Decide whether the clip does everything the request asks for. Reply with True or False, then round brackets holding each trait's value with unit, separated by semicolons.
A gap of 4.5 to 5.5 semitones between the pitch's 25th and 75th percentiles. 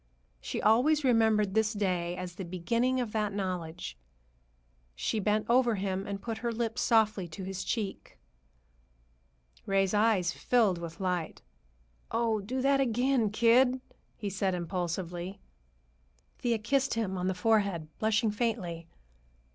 False (3.9 semitones)